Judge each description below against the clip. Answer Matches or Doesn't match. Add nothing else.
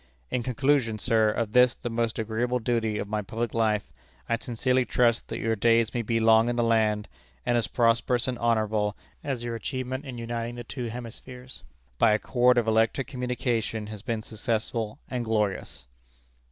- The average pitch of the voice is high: Doesn't match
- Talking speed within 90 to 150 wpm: Doesn't match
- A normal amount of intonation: Doesn't match